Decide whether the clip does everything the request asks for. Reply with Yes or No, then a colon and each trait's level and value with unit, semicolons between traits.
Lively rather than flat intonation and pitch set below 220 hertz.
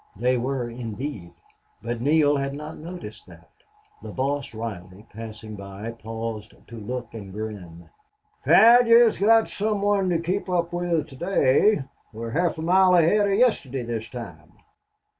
Yes: wide, 7.8 semitones; low, 135 Hz